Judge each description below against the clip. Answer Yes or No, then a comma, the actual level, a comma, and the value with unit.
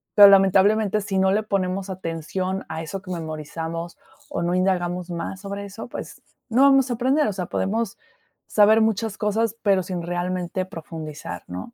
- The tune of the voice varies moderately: Yes, average, 3.2 semitones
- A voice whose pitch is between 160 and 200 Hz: Yes, high, 190 Hz